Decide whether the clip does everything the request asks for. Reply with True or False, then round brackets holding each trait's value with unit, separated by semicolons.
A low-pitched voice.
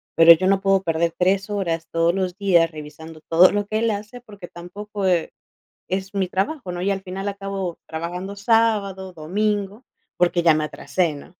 False (190 Hz)